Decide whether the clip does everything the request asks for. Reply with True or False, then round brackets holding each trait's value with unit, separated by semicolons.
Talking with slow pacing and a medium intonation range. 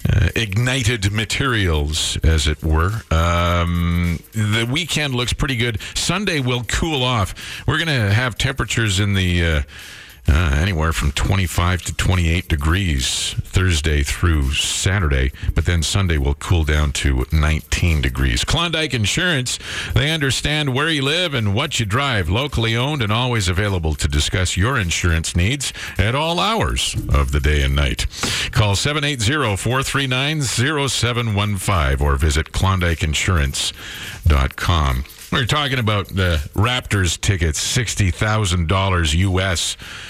False (130 wpm; 6.4 semitones)